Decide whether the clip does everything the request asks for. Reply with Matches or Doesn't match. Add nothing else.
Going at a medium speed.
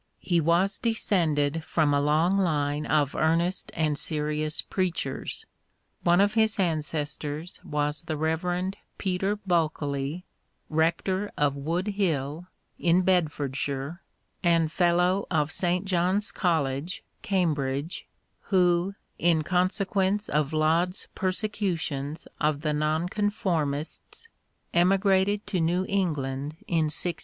Doesn't match